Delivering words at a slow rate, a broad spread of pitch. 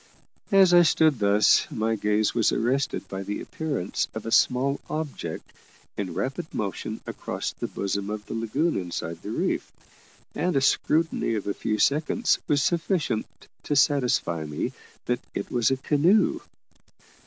No: average, 155 wpm; wide, 6.6 semitones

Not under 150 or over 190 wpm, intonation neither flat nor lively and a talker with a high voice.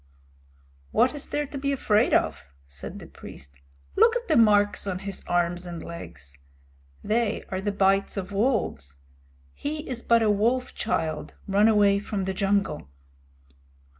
Yes: average, 155 wpm; average, 4.8 semitones; high, 205 Hz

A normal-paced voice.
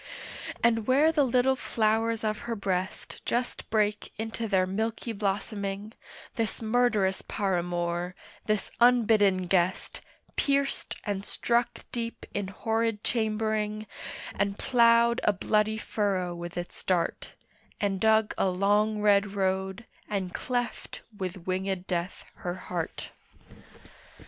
No: slow, 120 wpm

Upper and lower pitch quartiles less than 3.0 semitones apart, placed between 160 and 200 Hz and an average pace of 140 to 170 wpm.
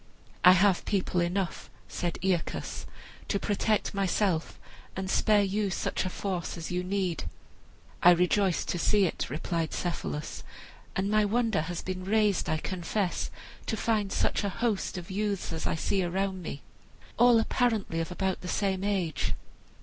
Yes: narrow, 2.6 semitones; high, 190 Hz; average, 155 wpm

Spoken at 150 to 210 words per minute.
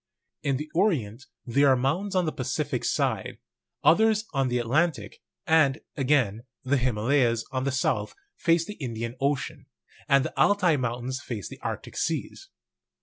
Yes: average, 155 wpm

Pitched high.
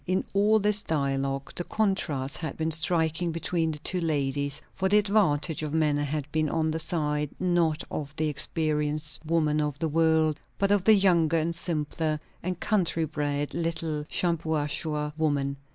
No: medium, 160 Hz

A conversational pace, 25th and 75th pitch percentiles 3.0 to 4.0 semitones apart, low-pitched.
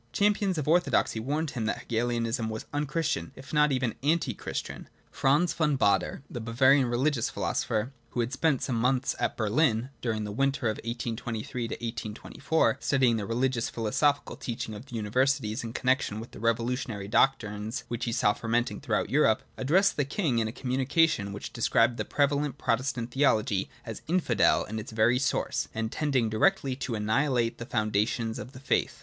Yes: average, 175 wpm; average, 3.6 semitones; low, 120 Hz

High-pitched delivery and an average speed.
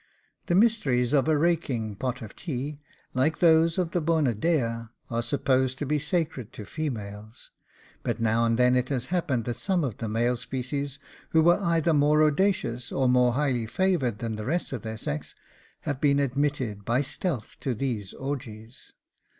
No: low, 130 Hz; average, 175 wpm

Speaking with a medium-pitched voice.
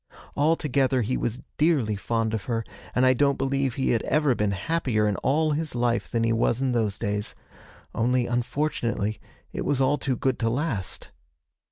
No: low, 125 Hz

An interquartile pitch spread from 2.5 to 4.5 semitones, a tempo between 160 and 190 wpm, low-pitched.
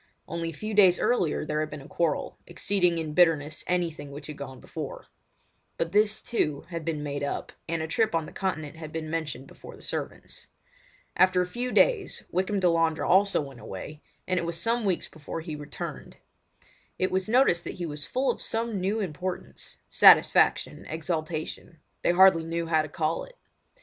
No: average, 3.5 semitones; average, 180 wpm; medium, 165 Hz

